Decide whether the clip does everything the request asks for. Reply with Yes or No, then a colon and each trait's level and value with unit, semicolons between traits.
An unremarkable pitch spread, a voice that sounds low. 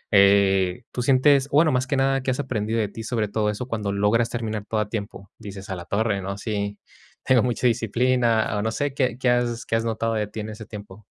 Yes: average, 3.3 semitones; low, 110 Hz